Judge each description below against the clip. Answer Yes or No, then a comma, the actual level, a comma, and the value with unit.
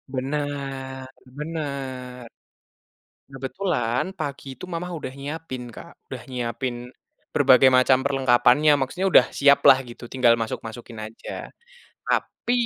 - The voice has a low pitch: Yes, low, 130 Hz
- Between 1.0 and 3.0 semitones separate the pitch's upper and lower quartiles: Yes, narrow, 2.4 semitones